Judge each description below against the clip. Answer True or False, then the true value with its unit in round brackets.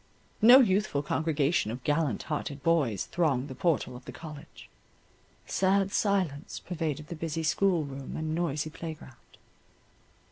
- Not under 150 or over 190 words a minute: False (135 wpm)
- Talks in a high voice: False (155 Hz)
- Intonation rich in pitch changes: False (3.4 semitones)